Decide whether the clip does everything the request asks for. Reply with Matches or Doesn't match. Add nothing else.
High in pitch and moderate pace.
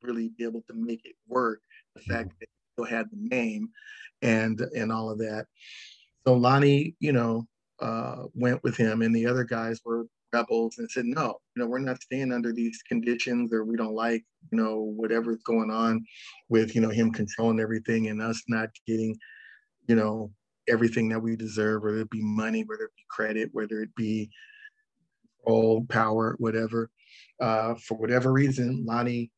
Doesn't match